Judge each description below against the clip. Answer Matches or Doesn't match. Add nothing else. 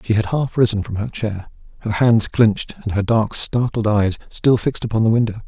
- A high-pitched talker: Doesn't match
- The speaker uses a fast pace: Matches